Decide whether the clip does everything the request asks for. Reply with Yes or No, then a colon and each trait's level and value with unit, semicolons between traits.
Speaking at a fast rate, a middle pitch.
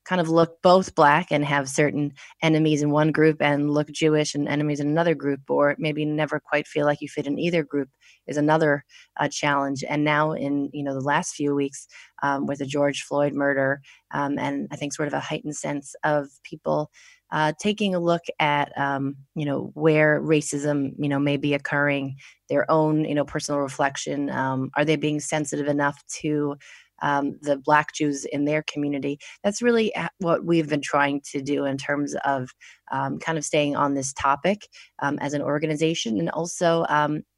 No: average, 195 wpm; medium, 145 Hz